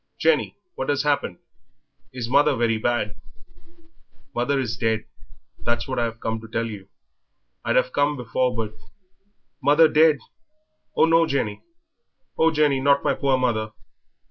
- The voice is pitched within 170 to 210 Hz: No, low, 130 Hz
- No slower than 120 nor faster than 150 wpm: Yes, average, 145 wpm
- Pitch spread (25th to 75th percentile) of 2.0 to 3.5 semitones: No, average, 4.3 semitones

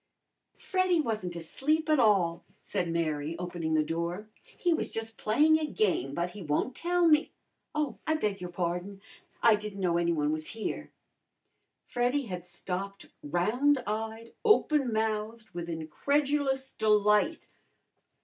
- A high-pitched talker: Yes, high, 210 Hz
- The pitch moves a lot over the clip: Yes, wide, 7.6 semitones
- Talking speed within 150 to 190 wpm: No, average, 140 wpm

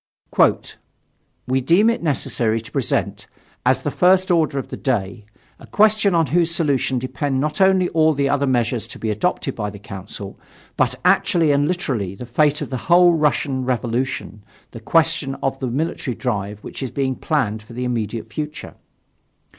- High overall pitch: No, low, 135 Hz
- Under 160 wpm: No, average, 170 wpm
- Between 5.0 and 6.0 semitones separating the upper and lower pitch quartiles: Yes, wide, 5.5 semitones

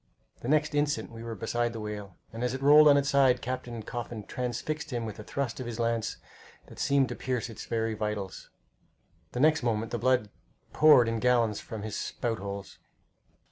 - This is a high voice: No, low, 120 Hz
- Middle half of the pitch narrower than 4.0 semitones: Yes, average, 3.0 semitones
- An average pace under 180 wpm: No, average, 195 wpm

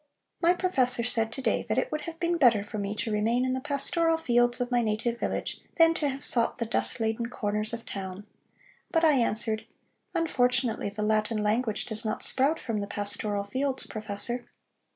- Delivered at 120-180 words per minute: No, average, 195 wpm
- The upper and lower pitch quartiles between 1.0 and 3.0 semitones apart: No, average, 3.8 semitones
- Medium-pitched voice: No, high, 235 Hz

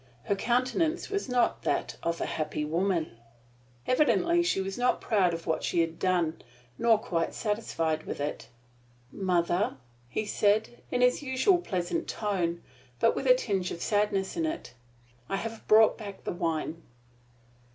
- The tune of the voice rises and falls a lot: Yes, wide, 6.4 semitones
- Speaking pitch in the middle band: No, high, 200 Hz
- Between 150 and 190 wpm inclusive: Yes, average, 155 wpm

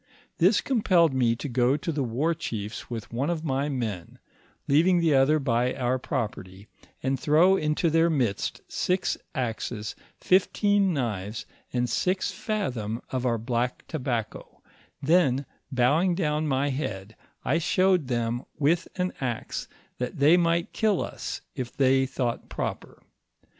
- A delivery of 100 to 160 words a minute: Yes, average, 145 wpm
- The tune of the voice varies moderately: No, wide, 5.7 semitones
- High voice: No, low, 135 Hz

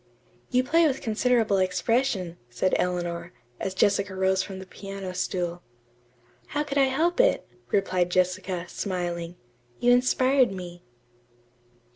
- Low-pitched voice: No, high, 190 Hz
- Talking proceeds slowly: Yes, slow, 125 wpm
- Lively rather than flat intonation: Yes, wide, 5.7 semitones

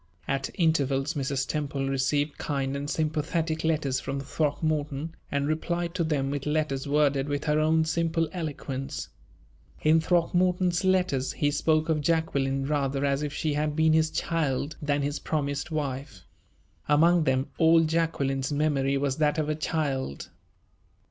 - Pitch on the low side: No, medium, 150 Hz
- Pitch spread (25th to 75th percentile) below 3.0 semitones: Yes, narrow, 2.5 semitones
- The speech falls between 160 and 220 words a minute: No, average, 150 wpm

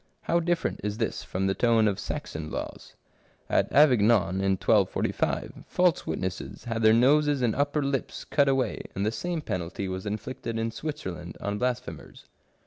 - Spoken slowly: No, average, 155 wpm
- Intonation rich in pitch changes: Yes, wide, 6.3 semitones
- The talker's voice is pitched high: No, low, 115 Hz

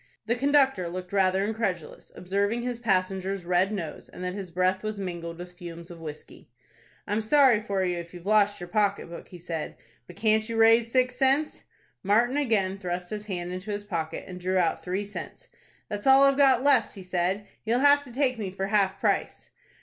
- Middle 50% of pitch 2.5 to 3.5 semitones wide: No, average, 4.0 semitones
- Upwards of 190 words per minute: Yes, average, 200 wpm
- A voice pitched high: Yes, high, 200 Hz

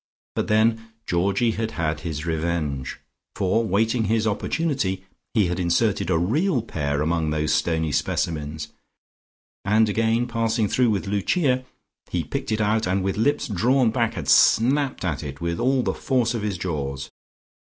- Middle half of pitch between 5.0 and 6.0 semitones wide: Yes, average, 5.3 semitones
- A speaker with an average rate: Yes, average, 160 wpm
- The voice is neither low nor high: No, low, 105 Hz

